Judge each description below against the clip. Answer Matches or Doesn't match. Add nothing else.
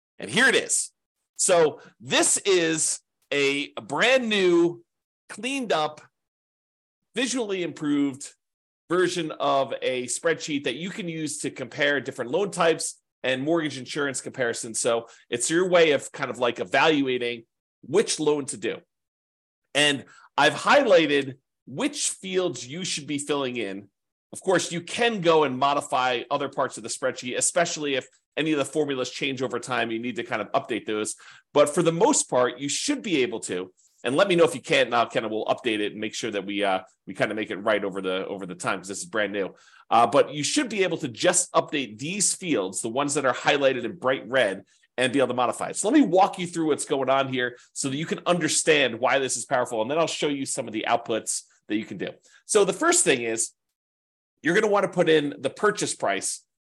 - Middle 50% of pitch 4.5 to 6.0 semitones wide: Matches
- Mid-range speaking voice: Matches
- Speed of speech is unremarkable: Doesn't match